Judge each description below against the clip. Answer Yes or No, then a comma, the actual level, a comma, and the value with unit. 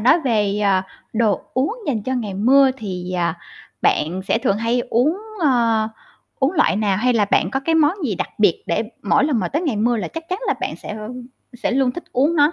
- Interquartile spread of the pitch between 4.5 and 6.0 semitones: Yes, average, 5.2 semitones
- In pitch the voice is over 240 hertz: No, high, 235 Hz